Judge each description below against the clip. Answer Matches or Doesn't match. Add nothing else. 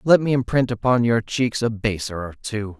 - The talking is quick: Matches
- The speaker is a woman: Doesn't match